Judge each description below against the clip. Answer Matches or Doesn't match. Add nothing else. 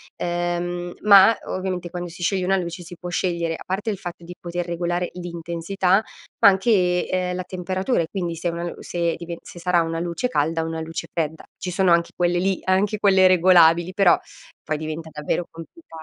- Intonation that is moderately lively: Doesn't match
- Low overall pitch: Doesn't match